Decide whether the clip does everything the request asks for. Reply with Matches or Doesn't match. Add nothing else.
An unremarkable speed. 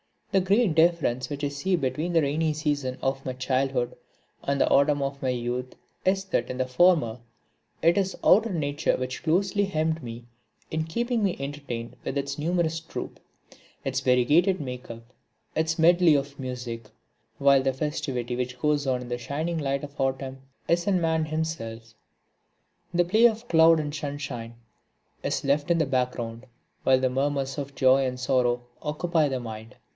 Matches